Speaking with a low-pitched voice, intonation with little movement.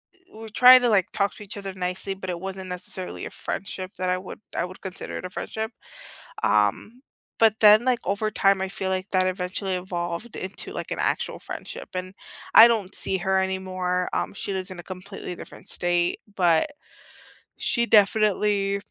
No: high, 190 Hz; narrow, 2.1 semitones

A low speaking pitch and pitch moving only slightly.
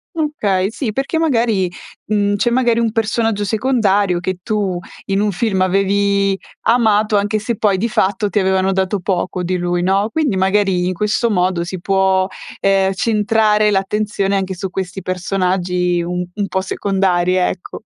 No: high, 195 Hz; narrow, 2.2 semitones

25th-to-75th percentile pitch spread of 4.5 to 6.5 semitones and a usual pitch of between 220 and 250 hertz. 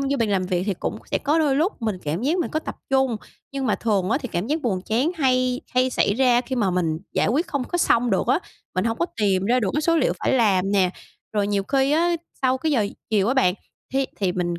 Yes: wide, 5.6 semitones; high, 240 Hz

